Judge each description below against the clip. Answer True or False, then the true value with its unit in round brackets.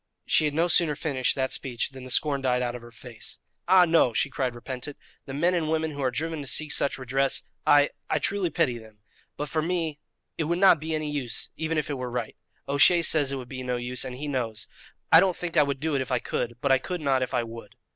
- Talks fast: True (255 wpm)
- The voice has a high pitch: False (140 Hz)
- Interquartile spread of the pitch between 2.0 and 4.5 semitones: True (4.0 semitones)